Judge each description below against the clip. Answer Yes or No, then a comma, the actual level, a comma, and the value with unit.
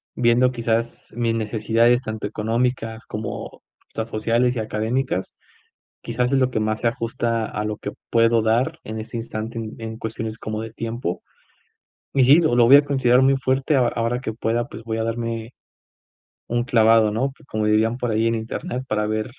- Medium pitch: No, low, 115 Hz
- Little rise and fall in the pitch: Yes, narrow, 1.8 semitones